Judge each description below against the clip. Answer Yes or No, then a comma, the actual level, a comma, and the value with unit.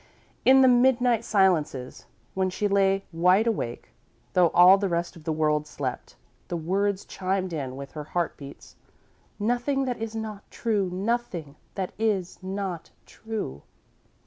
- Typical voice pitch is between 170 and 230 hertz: Yes, high, 190 Hz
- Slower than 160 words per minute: Yes, average, 145 wpm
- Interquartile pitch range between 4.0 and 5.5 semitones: Yes, average, 5.0 semitones